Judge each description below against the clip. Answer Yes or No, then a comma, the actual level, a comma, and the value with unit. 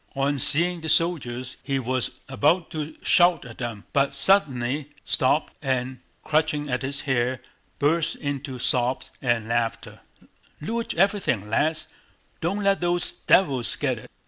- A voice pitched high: No, medium, 140 Hz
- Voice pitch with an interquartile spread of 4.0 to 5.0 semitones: Yes, average, 4.4 semitones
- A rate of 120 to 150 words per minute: Yes, average, 140 wpm